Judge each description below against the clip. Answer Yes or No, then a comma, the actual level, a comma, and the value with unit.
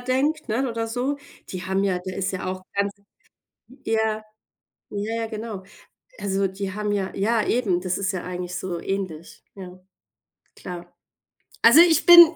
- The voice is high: Yes, high, 200 Hz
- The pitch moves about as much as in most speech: Yes, average, 3.6 semitones